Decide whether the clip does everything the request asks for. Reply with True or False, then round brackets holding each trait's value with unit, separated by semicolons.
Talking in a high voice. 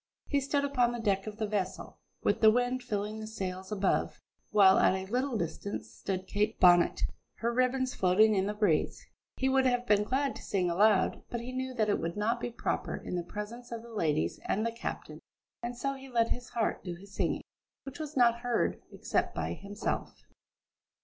True (220 Hz)